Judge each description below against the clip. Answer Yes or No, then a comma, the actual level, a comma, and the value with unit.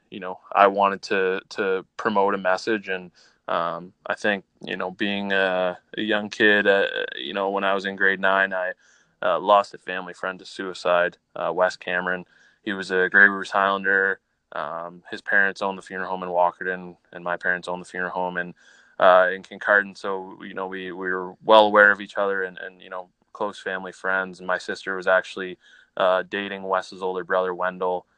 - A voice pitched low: Yes, very low, 95 Hz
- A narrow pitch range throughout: Yes, narrow, 1.4 semitones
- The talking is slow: No, average, 200 wpm